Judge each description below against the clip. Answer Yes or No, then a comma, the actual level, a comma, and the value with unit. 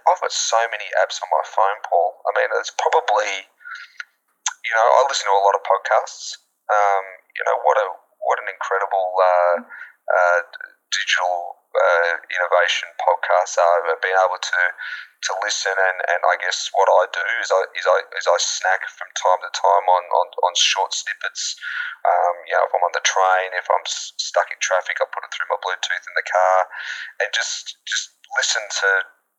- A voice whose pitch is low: Yes, low, 100 Hz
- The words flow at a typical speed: Yes, average, 190 wpm